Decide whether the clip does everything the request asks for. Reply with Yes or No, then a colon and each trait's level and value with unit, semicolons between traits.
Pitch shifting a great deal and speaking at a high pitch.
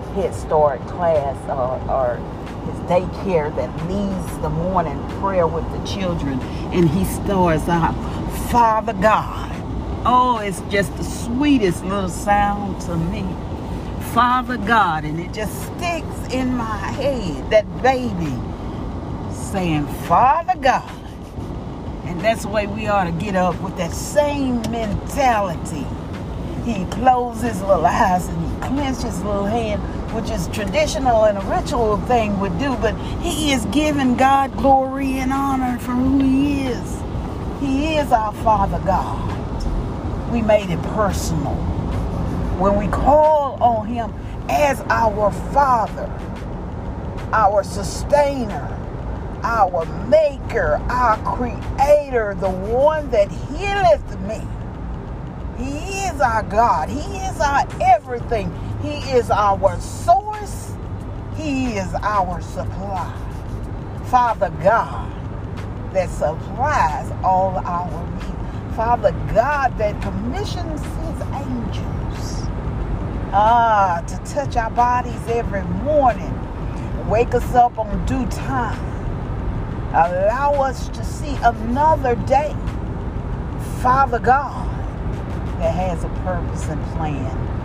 Yes: wide, 7.1 semitones; high, 240 Hz